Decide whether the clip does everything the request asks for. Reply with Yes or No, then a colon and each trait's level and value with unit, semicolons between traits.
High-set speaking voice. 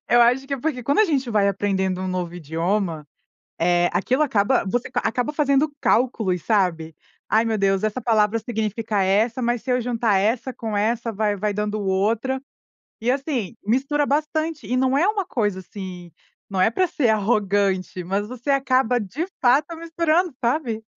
Yes: high, 225 Hz